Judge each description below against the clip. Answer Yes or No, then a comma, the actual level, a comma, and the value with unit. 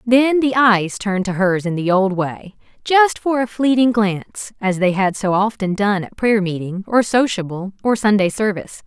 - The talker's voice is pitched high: Yes, high, 210 Hz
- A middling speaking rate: Yes, average, 195 wpm